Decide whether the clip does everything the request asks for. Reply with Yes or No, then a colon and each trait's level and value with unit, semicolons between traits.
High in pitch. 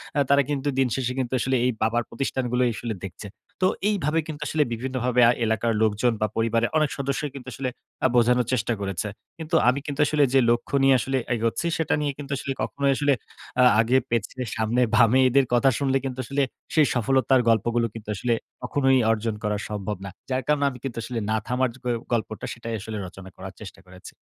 No: low, 125 Hz